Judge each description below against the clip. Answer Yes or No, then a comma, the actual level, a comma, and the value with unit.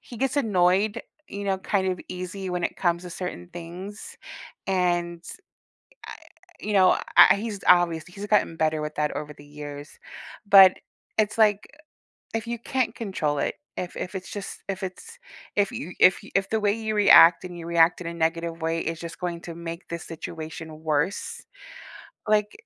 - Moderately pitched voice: Yes, medium, 180 Hz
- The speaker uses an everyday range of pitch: Yes, average, 3.4 semitones